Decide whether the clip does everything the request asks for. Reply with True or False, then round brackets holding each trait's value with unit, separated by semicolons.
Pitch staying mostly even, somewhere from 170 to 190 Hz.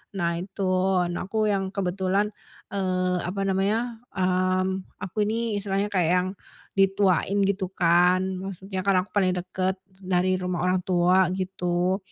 True (1.4 semitones; 185 Hz)